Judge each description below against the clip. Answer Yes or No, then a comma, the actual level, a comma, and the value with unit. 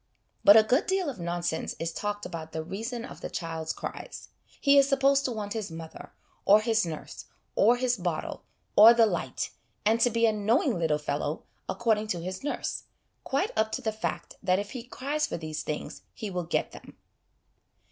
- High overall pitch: Yes, high, 215 Hz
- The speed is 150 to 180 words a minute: No, average, 195 wpm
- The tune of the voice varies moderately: No, wide, 6.0 semitones